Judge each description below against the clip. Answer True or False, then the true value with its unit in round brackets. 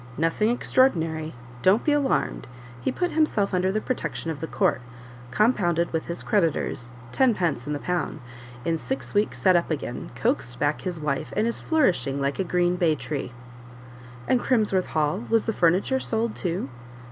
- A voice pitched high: False (175 Hz)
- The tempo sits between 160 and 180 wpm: True (170 wpm)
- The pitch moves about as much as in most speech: False (5.8 semitones)